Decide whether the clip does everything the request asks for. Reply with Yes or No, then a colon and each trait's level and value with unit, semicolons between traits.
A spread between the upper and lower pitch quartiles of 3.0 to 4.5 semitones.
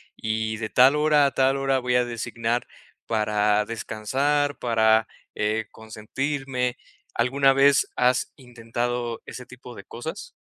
Yes: average, 3.4 semitones